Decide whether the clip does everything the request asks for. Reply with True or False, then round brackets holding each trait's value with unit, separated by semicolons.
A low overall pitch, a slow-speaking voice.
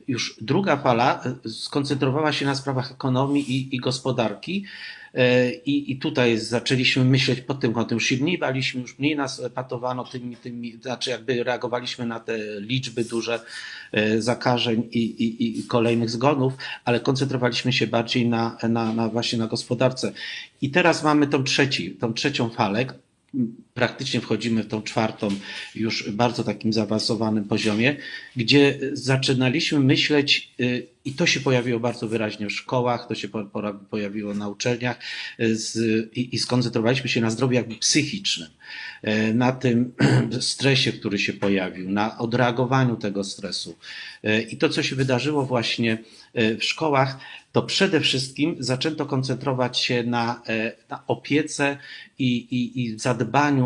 False (125 Hz; 135 wpm)